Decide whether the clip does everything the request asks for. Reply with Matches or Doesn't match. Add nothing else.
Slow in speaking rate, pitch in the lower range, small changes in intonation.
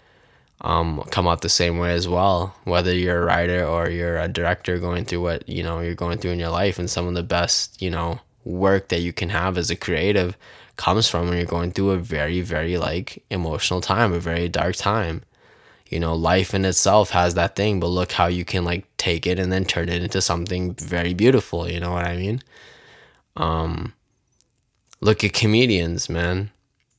Doesn't match